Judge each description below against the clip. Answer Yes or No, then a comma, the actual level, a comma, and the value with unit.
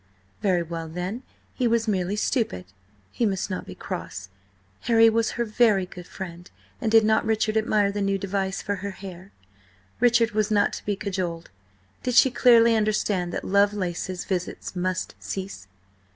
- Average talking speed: Yes, average, 165 wpm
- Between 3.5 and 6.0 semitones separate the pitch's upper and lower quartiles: No, average, 3.1 semitones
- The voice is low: No, high, 200 Hz